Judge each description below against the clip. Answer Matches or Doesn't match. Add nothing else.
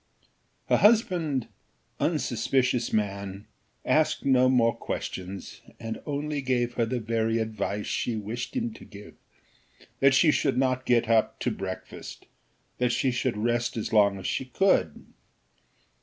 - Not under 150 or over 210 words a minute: Doesn't match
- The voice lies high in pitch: Doesn't match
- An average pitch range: Matches